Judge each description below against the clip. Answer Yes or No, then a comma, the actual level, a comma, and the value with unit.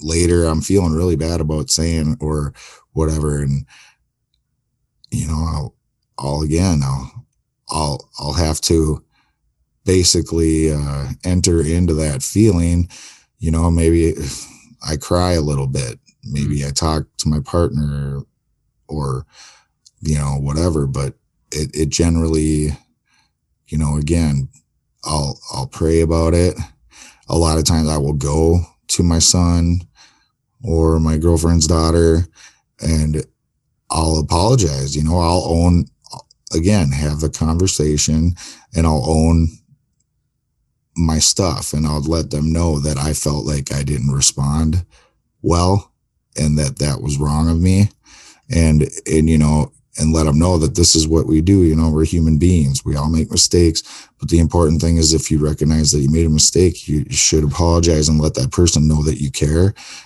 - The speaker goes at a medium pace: Yes, average, 155 wpm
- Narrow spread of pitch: Yes, narrow, 2.0 semitones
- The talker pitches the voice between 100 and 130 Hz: No, very low, 80 Hz